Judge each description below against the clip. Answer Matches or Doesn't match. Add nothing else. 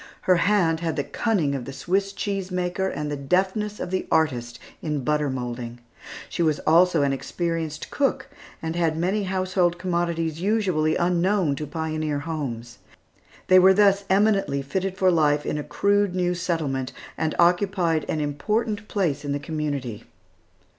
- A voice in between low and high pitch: Matches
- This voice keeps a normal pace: Matches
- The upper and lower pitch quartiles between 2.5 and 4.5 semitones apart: Matches